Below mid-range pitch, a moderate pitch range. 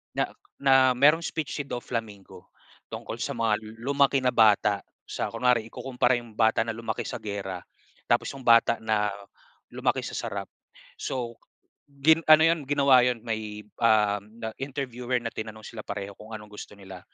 Yes: low, 115 Hz; average, 3.7 semitones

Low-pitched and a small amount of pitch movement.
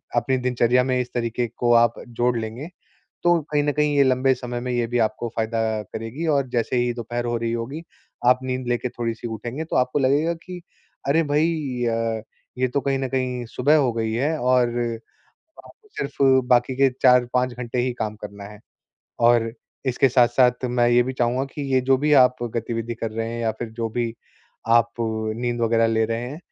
Yes: low, 120 Hz; narrow, 1.9 semitones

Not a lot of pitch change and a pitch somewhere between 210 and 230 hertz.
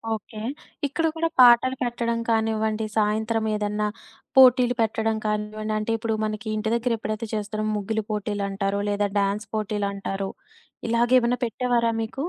Yes: narrow, 1.8 semitones; high, 220 Hz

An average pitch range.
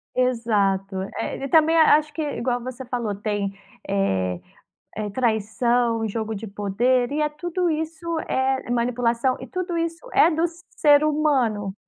No: wide, 6.1 semitones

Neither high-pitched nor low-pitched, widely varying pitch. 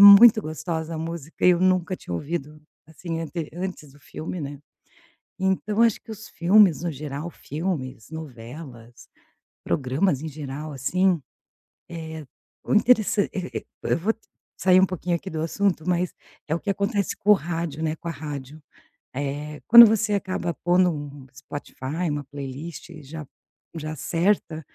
No: medium, 165 Hz; average, 4.0 semitones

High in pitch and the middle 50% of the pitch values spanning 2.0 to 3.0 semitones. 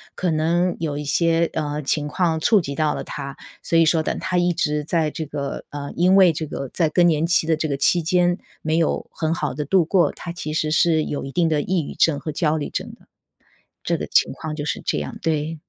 No: medium, 160 Hz; narrow, 2.4 semitones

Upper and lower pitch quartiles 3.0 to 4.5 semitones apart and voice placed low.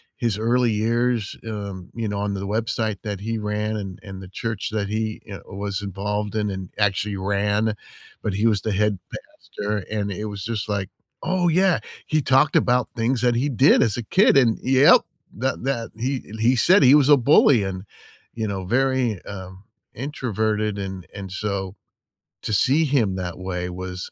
Yes: average, 3.4 semitones; low, 105 Hz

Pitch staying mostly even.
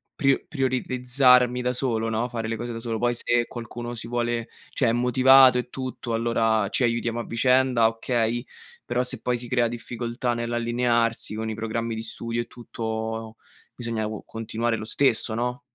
Yes: narrow, 1.5 semitones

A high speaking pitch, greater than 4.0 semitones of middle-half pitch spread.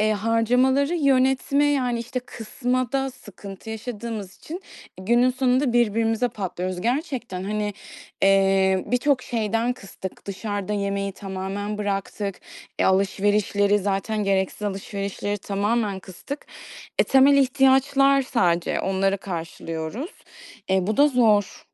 Yes: high, 215 Hz; average, 4.4 semitones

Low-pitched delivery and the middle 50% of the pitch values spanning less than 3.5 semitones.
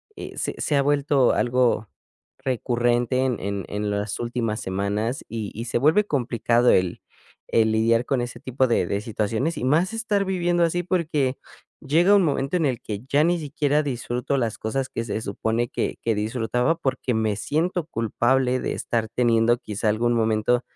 No: low, 120 Hz; average, 4.3 semitones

